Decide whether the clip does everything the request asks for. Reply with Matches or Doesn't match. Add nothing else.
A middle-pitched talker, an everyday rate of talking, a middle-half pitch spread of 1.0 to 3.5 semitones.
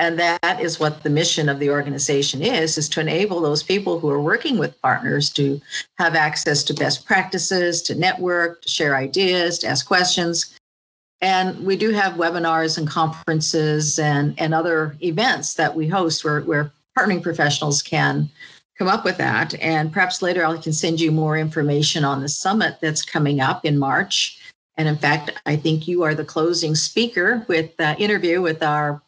Matches